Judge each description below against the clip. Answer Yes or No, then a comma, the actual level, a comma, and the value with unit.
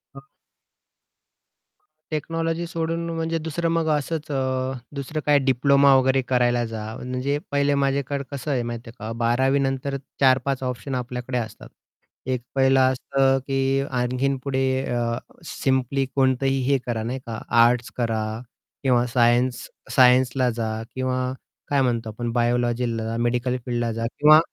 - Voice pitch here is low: Yes, low, 130 Hz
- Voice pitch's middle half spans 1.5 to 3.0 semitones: Yes, narrow, 2.4 semitones